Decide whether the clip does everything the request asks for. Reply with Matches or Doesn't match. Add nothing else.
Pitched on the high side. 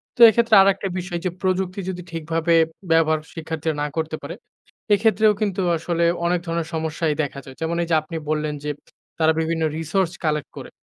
Doesn't match